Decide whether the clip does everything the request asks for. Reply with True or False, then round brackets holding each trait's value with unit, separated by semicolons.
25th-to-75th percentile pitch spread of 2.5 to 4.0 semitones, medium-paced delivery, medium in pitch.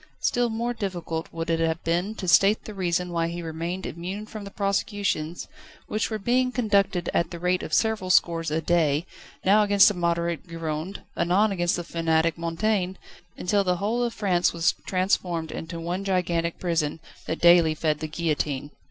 True (3.2 semitones; 180 wpm; 175 Hz)